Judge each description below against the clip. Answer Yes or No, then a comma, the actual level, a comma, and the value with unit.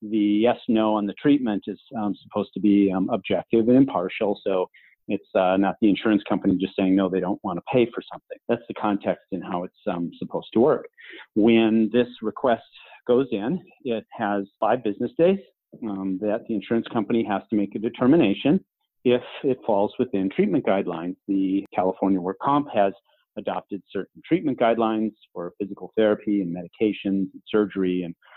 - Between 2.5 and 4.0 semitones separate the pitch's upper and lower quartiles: Yes, average, 3.0 semitones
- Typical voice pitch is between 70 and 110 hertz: Yes, low, 105 Hz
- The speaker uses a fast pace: No, average, 180 wpm